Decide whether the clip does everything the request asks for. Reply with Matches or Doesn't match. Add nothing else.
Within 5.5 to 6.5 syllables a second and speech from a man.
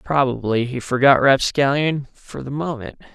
Doesn't match